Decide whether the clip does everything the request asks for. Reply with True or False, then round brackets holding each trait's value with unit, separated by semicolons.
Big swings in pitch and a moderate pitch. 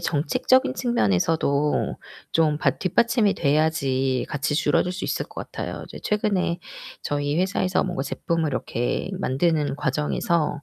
False (4.3 semitones; 160 Hz)